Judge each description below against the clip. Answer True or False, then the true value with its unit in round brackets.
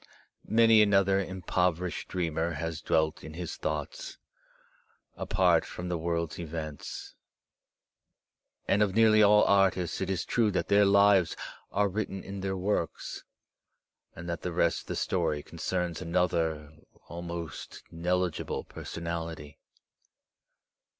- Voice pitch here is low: True (90 Hz)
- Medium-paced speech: False (120 wpm)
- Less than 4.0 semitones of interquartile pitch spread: True (2.9 semitones)